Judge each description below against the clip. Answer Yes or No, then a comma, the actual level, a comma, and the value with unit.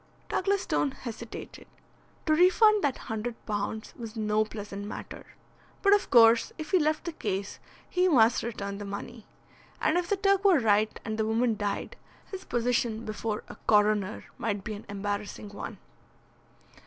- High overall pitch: Yes, high, 225 Hz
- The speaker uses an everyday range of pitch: No, wide, 6.8 semitones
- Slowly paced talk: No, average, 160 wpm